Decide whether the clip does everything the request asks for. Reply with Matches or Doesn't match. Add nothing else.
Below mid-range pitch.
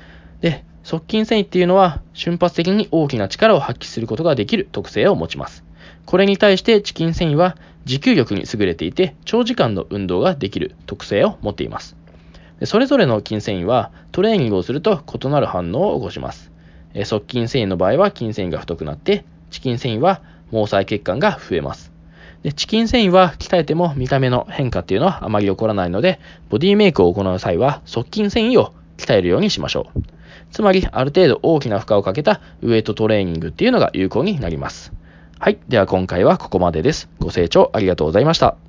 Matches